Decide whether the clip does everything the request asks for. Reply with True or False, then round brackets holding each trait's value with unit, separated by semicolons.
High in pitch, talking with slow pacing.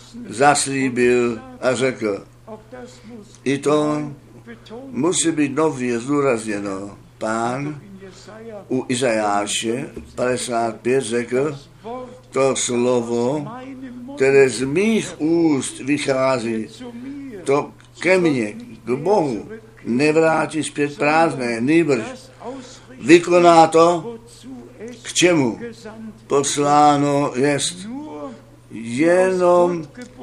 False (140 Hz; 75 wpm)